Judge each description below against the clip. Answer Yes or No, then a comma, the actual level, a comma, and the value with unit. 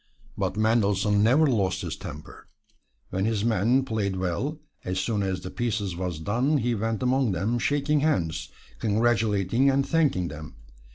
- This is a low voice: Yes, low, 110 Hz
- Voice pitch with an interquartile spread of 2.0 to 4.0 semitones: No, average, 4.9 semitones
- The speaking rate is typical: Yes, average, 155 wpm